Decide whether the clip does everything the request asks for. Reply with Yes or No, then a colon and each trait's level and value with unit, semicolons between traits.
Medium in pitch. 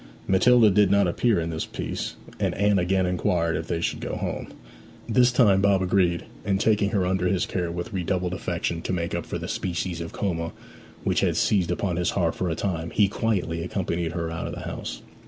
No: very low, 90 Hz